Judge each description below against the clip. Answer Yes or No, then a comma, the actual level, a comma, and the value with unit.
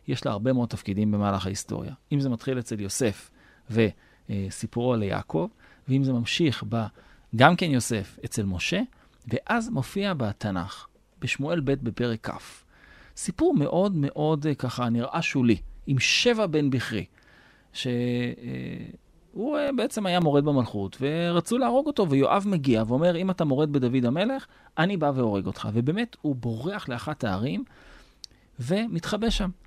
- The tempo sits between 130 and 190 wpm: Yes, average, 135 wpm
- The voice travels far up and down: Yes, wide, 7.0 semitones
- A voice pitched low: Yes, low, 130 Hz